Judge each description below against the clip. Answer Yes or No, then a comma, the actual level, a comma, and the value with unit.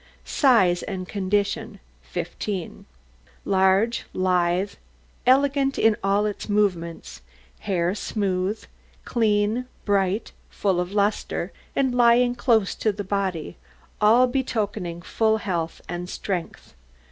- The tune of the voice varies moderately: Yes, average, 3.3 semitones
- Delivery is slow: Yes, slow, 105 wpm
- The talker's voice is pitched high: Yes, high, 205 Hz